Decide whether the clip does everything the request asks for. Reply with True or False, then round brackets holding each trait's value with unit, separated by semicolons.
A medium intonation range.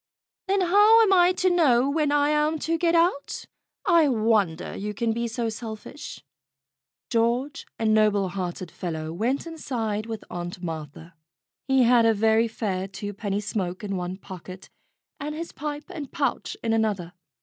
False (7.0 semitones)